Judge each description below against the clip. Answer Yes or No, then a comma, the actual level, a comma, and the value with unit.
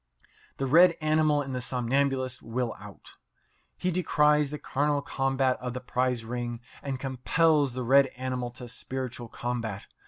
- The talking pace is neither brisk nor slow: Yes, average, 150 wpm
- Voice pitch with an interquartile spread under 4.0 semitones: Yes, narrow, 2.6 semitones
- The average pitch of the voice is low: Yes, low, 130 Hz